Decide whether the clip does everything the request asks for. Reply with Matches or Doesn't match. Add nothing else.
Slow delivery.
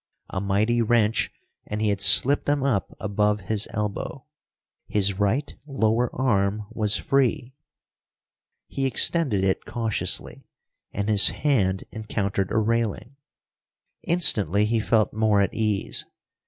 Matches